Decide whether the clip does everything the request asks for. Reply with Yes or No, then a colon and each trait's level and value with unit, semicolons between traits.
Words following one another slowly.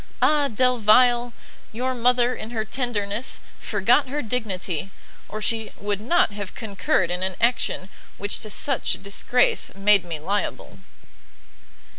Yes: slow, 130 wpm